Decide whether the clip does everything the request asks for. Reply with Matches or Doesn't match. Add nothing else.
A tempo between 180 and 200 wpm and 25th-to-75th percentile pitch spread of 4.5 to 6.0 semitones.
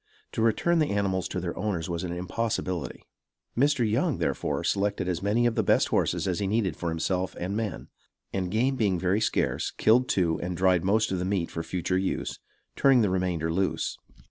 Doesn't match